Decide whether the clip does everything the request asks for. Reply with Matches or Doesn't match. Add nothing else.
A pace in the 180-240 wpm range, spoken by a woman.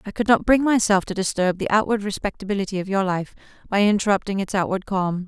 Matches